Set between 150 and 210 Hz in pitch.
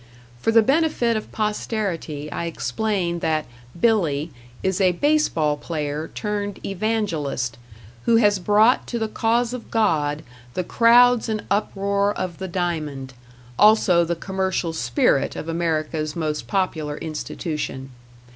Yes: medium, 185 Hz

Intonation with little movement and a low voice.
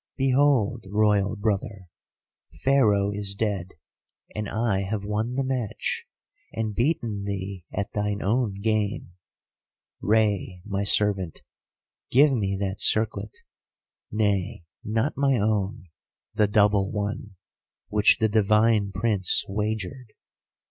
Yes: narrow, 2.0 semitones; low, 105 Hz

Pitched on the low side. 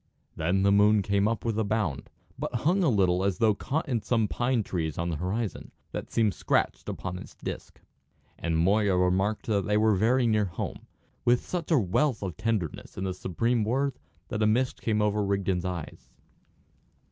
Yes: low, 105 Hz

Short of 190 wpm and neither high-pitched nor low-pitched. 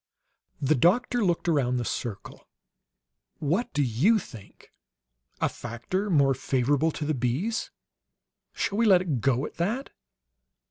Yes: slow, 135 wpm; medium, 150 Hz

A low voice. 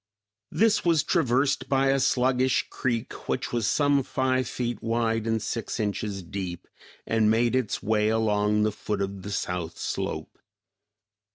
Yes: low, 115 Hz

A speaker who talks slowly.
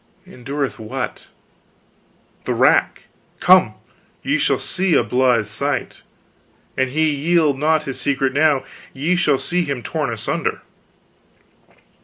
Yes: slow, 120 wpm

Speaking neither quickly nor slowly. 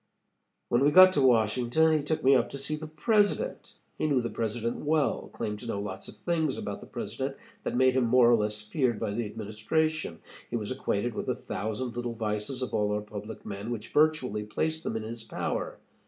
No: fast, 215 wpm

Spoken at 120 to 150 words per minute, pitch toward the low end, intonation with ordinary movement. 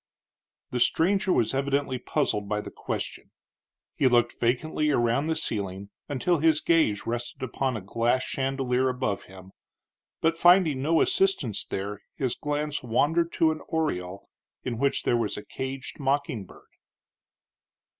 Yes: average, 145 wpm; low, 130 Hz; average, 4.8 semitones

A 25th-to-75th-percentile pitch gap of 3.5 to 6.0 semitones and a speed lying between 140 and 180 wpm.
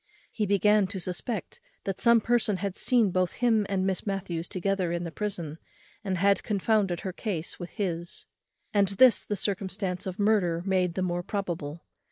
No: average, 2.7 semitones; average, 175 wpm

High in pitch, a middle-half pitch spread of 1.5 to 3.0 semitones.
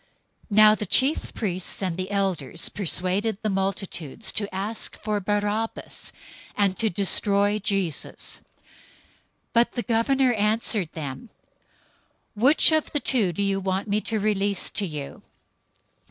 Yes: high, 205 Hz; narrow, 2.5 semitones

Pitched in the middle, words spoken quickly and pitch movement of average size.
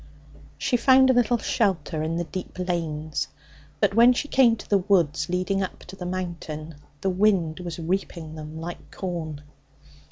No: medium, 180 Hz; average, 165 wpm; average, 3.9 semitones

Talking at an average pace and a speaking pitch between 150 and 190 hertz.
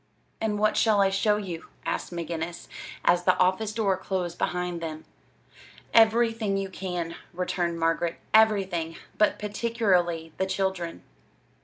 No: slow, 130 wpm; medium, 185 Hz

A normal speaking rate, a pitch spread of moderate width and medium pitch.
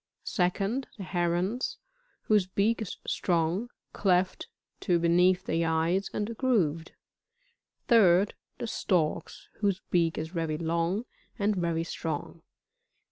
No: slow, 115 wpm; average, 3.5 semitones; medium, 180 Hz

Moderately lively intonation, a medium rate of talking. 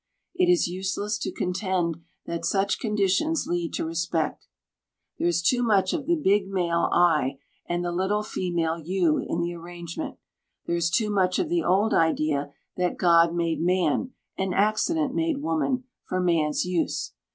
Yes: average, 3.7 semitones; average, 165 wpm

